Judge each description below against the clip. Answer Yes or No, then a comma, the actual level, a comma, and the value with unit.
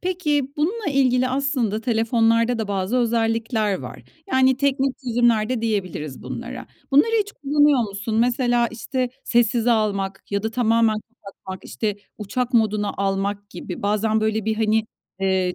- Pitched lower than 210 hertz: No, high, 230 Hz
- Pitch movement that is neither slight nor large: Yes, average, 3.3 semitones